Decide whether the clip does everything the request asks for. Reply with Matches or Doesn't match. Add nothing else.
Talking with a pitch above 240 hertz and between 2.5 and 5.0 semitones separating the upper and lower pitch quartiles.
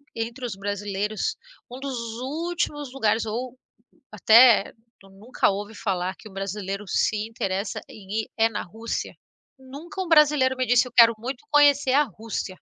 Doesn't match